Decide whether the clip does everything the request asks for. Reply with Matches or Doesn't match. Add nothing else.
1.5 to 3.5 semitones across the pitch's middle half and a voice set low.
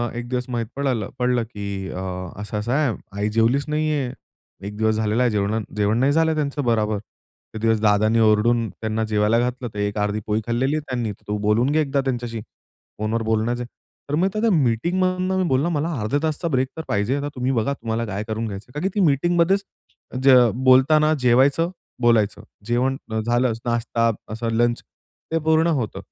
Doesn't match